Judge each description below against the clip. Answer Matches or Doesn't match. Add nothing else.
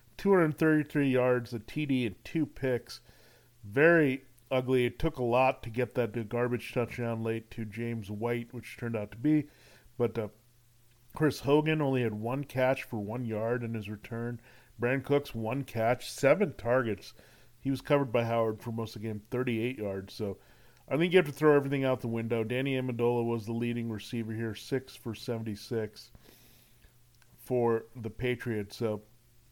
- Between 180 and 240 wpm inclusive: Doesn't match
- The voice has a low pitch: Matches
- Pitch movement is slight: Matches